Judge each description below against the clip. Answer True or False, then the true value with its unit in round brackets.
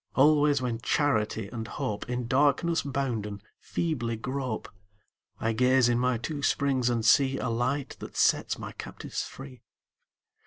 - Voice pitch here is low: True (125 Hz)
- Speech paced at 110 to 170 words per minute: True (145 wpm)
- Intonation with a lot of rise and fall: False (3.5 semitones)